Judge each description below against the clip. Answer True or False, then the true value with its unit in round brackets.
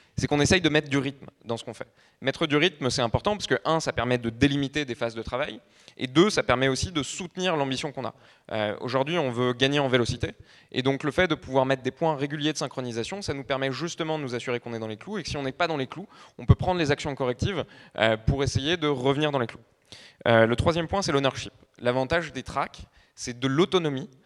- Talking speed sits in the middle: False (255 wpm)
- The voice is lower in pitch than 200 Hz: True (135 Hz)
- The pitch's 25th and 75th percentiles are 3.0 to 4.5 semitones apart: True (4.0 semitones)